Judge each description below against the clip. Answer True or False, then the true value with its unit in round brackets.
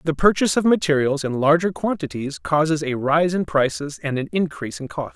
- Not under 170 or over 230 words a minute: True (200 wpm)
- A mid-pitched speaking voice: True (150 Hz)